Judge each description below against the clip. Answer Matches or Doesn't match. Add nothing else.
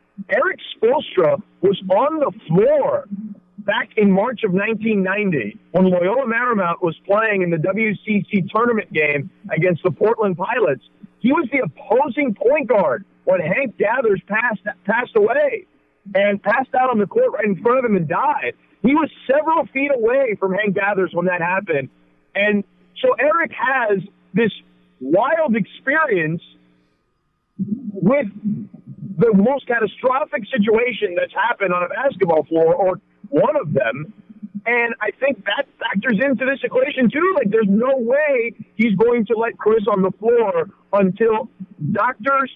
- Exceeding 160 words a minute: Doesn't match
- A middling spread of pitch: Doesn't match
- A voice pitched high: Matches